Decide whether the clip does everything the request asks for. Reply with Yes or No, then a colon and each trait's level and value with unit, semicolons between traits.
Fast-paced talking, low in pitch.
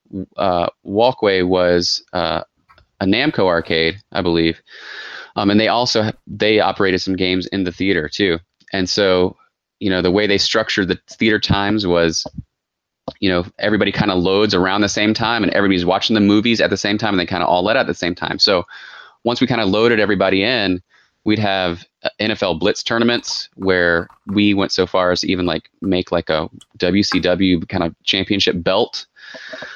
No: average, 190 wpm; very low, 95 Hz